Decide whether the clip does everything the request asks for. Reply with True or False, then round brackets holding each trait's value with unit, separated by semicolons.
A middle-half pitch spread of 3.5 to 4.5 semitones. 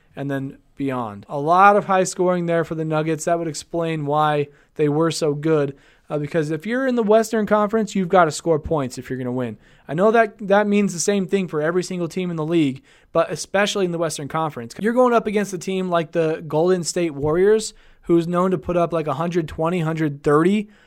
True (3.8 semitones)